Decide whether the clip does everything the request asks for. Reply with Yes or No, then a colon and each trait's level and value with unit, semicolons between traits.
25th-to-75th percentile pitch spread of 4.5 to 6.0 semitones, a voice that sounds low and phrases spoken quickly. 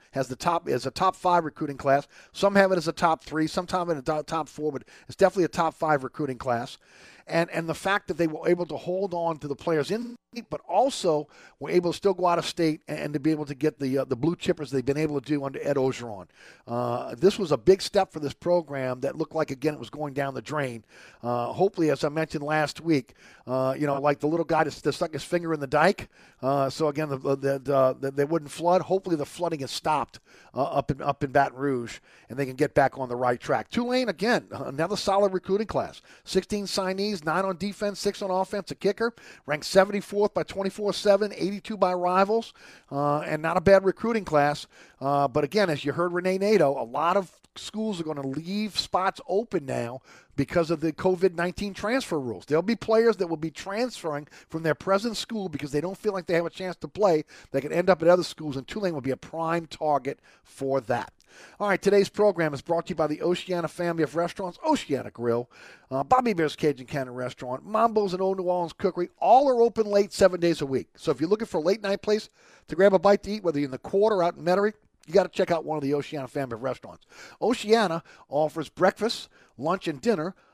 No: average, 5.1 semitones; medium, 165 Hz; fast, 240 wpm